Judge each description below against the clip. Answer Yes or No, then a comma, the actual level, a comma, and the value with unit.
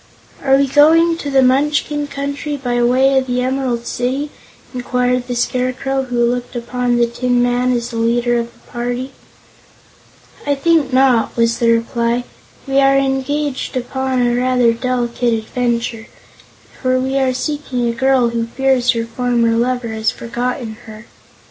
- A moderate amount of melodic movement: No, narrow, 2.0 semitones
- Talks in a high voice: Yes, very high, 250 Hz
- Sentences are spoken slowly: No, average, 155 wpm